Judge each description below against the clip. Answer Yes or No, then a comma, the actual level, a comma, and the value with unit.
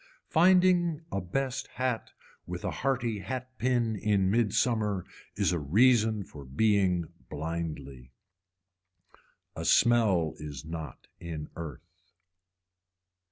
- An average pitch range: No, wide, 6.6 semitones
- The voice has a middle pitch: No, low, 100 Hz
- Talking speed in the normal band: No, slow, 105 wpm